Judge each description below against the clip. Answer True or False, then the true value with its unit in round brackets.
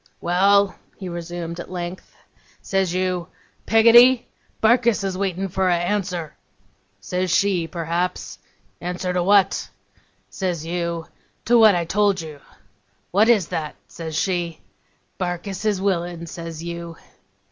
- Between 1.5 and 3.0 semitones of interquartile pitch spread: True (2.6 semitones)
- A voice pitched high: False (180 Hz)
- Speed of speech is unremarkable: False (125 wpm)